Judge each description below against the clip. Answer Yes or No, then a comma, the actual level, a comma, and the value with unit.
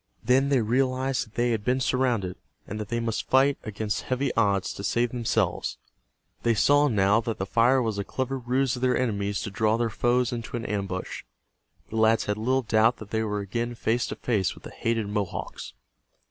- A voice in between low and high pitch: No, low, 115 Hz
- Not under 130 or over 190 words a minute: No, average, 200 wpm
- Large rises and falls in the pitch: No, average, 3.1 semitones